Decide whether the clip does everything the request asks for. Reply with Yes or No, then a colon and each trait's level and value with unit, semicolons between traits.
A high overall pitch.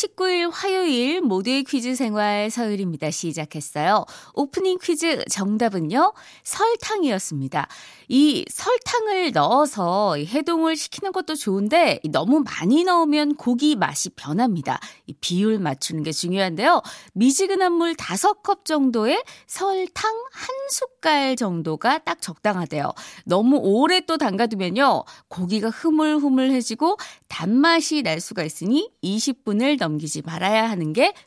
Yes: very high, 270 Hz